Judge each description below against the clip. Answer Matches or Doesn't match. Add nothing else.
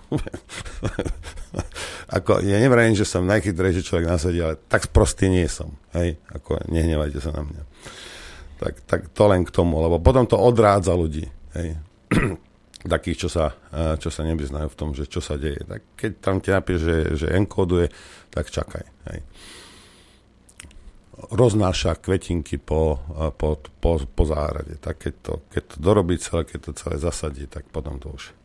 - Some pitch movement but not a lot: Matches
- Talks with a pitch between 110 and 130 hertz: Doesn't match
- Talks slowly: Doesn't match